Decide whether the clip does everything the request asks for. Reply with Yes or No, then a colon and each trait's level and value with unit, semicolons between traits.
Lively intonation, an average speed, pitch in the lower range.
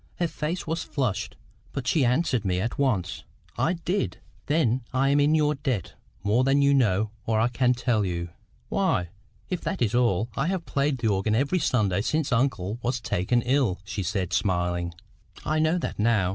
Yes: wide, 5.8 semitones; average, 185 wpm; low, 125 Hz